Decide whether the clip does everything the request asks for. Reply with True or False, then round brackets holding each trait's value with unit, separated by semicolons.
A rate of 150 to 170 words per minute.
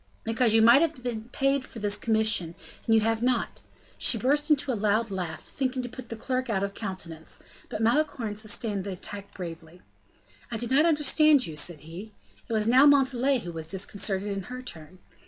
False (200 wpm)